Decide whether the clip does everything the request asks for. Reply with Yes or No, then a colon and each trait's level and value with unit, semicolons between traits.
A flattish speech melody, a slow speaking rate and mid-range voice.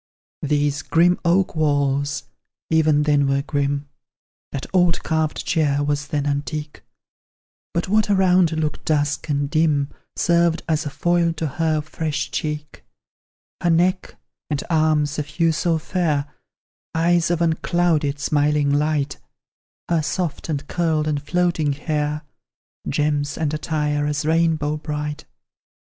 Yes: narrow, 2.1 semitones; slow, 130 wpm; medium, 155 Hz